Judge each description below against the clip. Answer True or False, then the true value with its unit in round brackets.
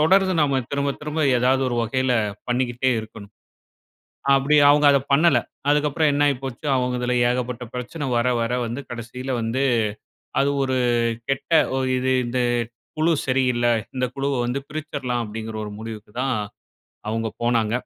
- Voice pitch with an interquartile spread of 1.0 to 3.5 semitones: True (2.8 semitones)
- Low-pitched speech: True (130 Hz)